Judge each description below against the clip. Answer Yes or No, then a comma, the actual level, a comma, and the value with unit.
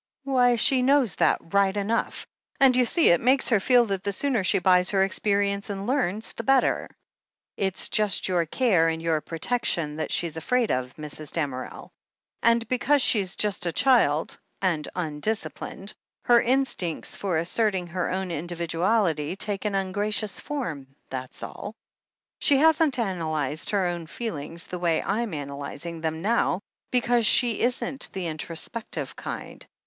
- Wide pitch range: Yes, wide, 6.0 semitones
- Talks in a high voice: Yes, high, 195 Hz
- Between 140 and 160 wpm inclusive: Yes, average, 155 wpm